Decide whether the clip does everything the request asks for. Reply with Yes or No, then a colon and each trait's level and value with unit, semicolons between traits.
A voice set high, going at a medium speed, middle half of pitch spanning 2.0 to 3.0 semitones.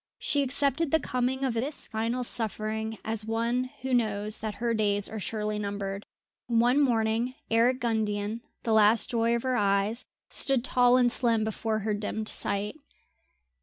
Yes: high, 225 Hz; average, 160 wpm; narrow, 2.5 semitones